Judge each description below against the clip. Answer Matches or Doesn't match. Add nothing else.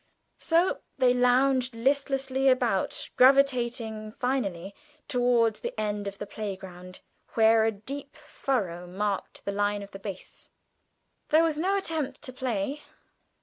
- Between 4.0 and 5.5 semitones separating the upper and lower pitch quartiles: Matches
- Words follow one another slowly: Matches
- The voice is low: Doesn't match